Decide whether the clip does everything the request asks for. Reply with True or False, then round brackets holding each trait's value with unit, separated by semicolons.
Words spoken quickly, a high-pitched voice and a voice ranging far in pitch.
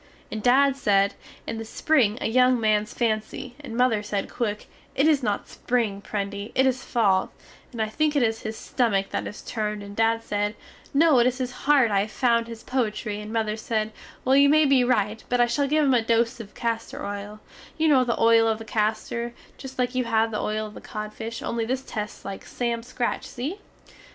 False (215 wpm; 230 Hz; 3.0 semitones)